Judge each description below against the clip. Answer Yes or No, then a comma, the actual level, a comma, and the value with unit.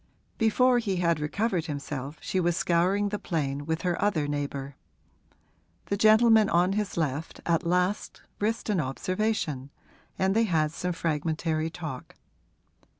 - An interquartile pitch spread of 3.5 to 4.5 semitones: No, average, 4.9 semitones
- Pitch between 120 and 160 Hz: No, medium, 170 Hz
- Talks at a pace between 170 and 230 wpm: No, average, 140 wpm